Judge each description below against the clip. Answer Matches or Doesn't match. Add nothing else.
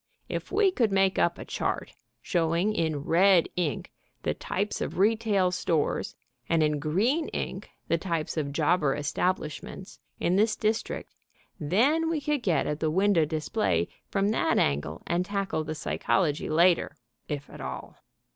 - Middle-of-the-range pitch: Matches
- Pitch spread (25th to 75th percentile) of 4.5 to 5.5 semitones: Matches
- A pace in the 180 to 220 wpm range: Doesn't match